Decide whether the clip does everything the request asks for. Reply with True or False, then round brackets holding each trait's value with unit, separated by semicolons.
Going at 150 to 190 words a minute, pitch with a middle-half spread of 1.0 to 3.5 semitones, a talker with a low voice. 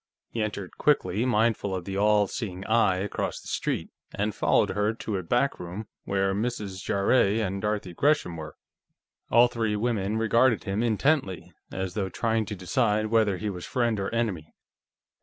True (170 wpm; 2.9 semitones; 105 Hz)